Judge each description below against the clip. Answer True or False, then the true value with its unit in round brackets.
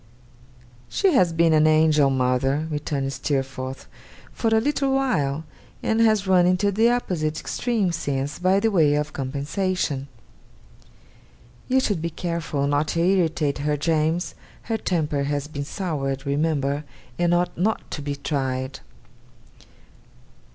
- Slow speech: True (130 wpm)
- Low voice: False (155 Hz)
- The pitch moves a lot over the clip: False (4.7 semitones)